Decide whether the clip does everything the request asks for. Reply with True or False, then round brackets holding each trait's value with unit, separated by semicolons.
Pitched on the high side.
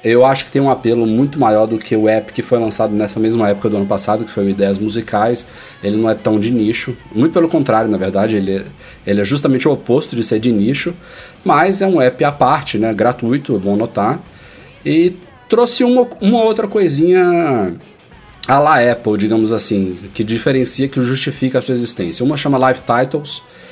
False (120 Hz)